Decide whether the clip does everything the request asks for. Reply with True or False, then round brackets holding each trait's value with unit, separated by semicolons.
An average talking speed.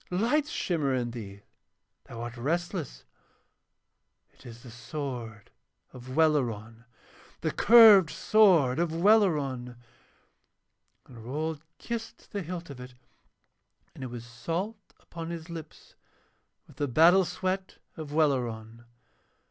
False (115 wpm)